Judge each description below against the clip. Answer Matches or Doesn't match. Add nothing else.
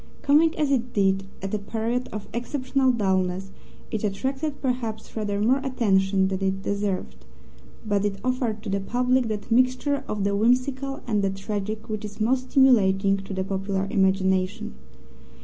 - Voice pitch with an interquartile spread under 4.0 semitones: Doesn't match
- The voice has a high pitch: Matches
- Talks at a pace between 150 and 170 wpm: Matches